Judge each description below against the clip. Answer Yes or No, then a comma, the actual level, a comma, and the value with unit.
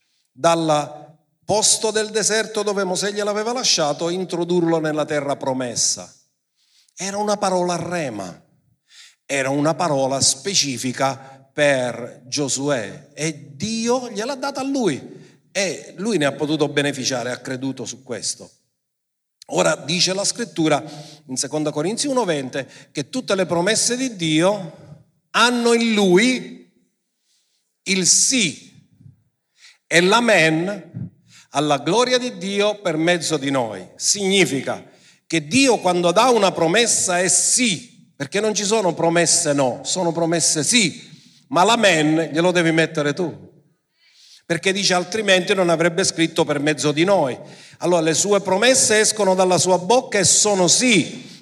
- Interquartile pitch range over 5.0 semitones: Yes, wide, 5.4 semitones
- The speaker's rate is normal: Yes, average, 130 wpm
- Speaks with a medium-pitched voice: Yes, medium, 175 Hz